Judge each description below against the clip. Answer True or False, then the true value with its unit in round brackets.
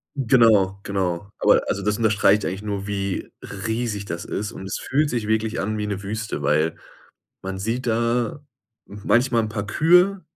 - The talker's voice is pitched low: True (105 Hz)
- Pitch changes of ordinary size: True (3.0 semitones)